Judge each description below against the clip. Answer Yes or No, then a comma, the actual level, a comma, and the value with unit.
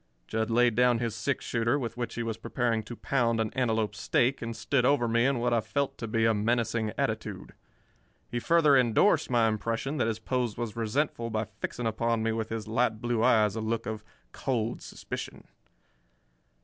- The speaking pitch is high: No, low, 115 Hz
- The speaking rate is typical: Yes, average, 190 wpm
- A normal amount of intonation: No, narrow, 1.7 semitones